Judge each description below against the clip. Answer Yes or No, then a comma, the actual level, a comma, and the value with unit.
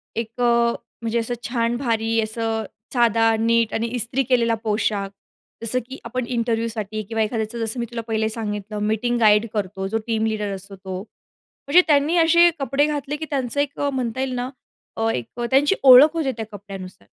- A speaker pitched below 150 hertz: No, high, 230 Hz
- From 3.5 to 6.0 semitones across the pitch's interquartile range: No, average, 2.7 semitones